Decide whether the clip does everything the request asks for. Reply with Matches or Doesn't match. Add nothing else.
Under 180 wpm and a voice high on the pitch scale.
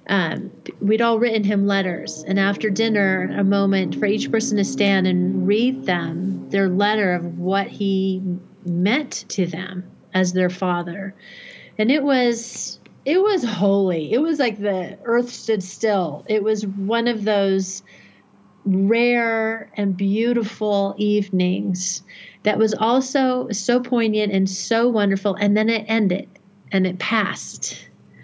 Matches